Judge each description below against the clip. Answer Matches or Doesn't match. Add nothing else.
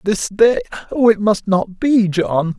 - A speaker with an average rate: Matches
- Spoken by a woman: Doesn't match